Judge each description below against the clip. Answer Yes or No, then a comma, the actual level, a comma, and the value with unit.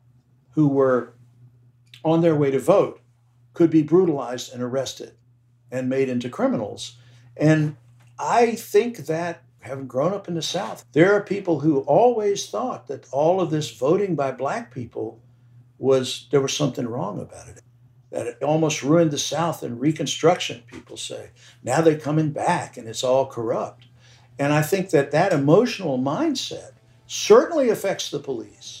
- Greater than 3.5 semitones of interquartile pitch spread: Yes, average, 4.9 semitones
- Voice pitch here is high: No, low, 135 Hz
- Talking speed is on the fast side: No, average, 160 wpm